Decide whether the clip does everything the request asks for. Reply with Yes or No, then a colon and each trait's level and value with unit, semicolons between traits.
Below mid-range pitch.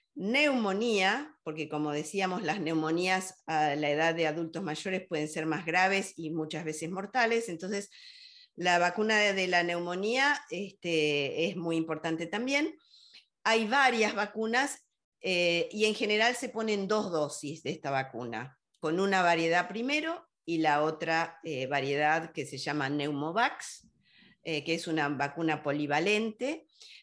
No: medium, 175 Hz